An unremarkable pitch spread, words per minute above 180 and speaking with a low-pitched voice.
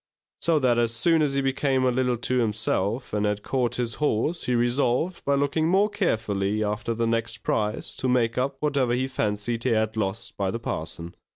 Yes: average, 3.8 semitones; average, 200 wpm; low, 120 Hz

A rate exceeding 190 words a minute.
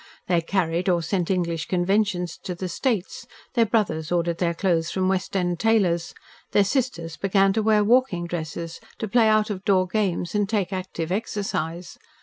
No: average, 170 wpm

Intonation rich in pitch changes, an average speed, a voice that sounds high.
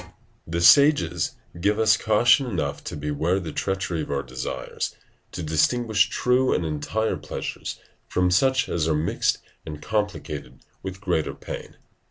No: wide, 5.8 semitones; average, 155 wpm; very low, 90 Hz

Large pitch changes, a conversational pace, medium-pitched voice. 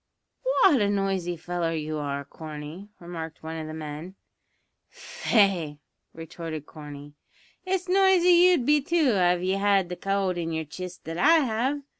Yes: wide, 6.5 semitones; average, 155 wpm; medium, 180 Hz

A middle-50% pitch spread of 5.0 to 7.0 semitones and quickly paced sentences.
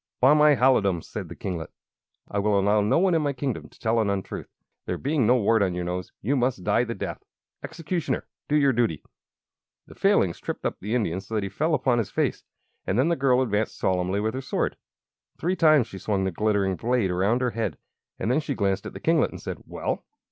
Yes: wide, 5.5 semitones; fast, 225 wpm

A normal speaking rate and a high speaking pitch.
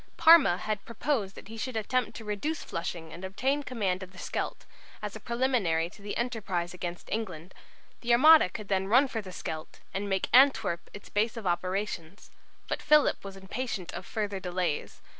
Yes: average, 180 wpm; high, 200 Hz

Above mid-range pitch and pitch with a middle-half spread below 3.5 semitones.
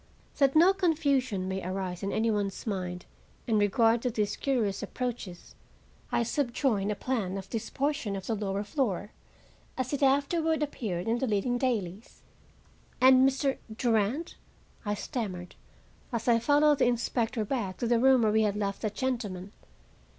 No: high, 230 Hz; average, 4.7 semitones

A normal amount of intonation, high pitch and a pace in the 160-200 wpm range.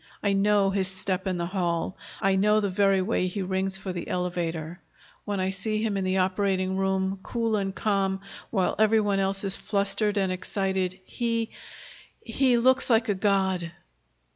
No: narrow, 1.7 semitones; high, 195 Hz; average, 175 wpm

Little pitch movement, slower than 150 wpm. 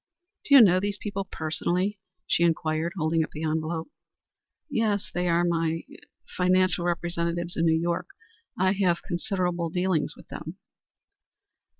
Yes: narrow, 2.2 semitones; average, 140 wpm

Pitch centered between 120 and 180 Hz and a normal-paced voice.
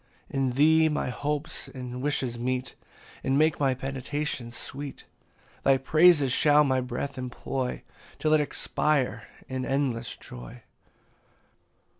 No: low, 135 Hz; slow, 125 wpm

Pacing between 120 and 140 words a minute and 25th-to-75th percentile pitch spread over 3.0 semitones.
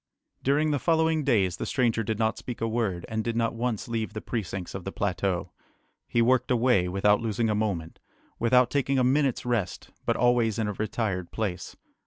No: average, 195 wpm; average, 3.6 semitones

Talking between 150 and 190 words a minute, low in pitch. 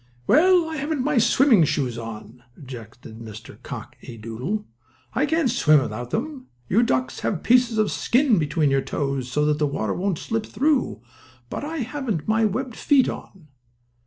No: average, 165 wpm; high, 195 Hz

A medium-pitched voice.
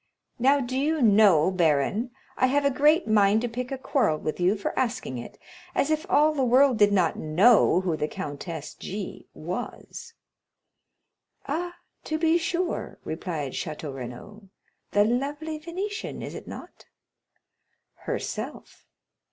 No: high, 230 Hz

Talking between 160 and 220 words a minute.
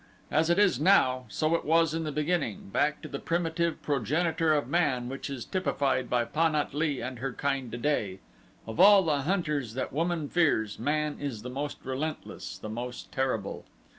Yes: average, 185 wpm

